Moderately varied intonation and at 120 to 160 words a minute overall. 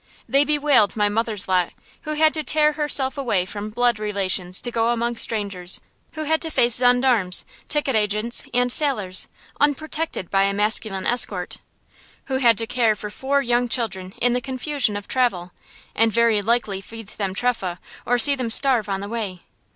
No: average, 4.4 semitones; average, 175 wpm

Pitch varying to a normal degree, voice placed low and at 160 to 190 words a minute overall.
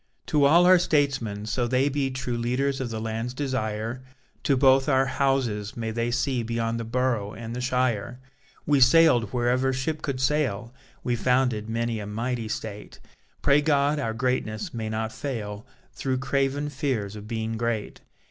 Yes: average, 3.3 semitones; low, 125 Hz; average, 165 wpm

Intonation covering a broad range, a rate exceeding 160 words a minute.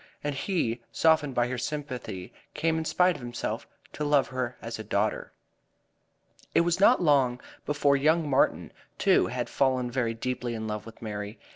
No: average, 4.2 semitones; average, 170 wpm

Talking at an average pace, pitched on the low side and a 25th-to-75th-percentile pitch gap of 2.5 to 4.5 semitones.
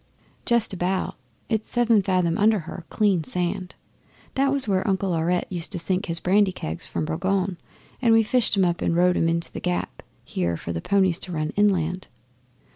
No: average, 190 wpm; medium, 185 Hz; average, 3.3 semitones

